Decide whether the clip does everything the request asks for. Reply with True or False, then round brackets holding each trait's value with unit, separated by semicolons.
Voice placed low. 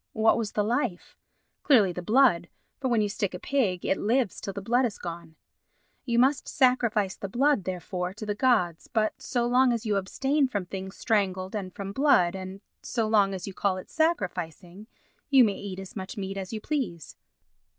False (205 Hz)